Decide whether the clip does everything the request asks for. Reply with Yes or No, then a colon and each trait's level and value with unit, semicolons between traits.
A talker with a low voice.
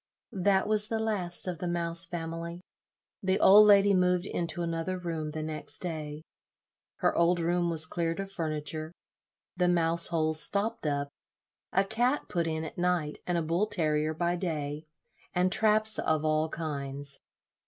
No: medium, 170 Hz